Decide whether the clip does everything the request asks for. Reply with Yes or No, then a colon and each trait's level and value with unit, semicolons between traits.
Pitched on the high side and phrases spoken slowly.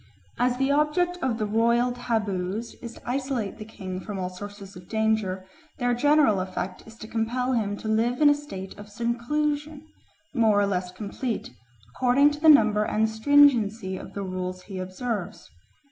No: high, 225 Hz; average, 175 wpm